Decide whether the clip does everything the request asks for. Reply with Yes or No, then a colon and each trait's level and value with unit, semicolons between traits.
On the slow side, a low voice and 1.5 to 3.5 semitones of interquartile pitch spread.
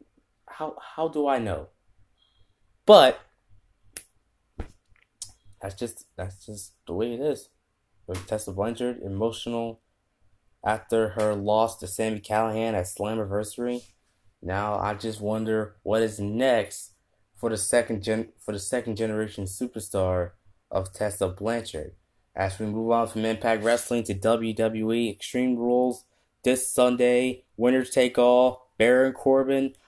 Yes: slow, 125 wpm; low, 110 Hz; average, 2.9 semitones